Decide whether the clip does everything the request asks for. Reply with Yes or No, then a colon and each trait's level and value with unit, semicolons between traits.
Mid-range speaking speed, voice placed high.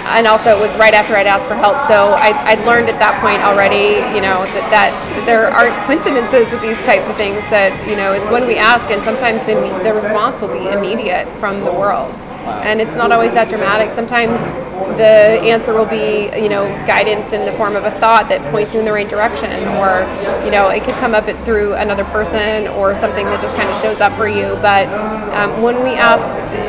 No: fast, 225 wpm; high, 215 Hz